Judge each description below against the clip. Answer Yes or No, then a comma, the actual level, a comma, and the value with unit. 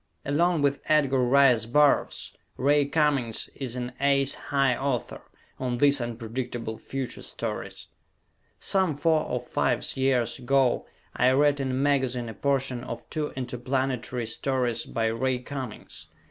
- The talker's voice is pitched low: Yes, low, 130 Hz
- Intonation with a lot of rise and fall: No, narrow, 2.5 semitones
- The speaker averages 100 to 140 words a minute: Yes, slow, 135 wpm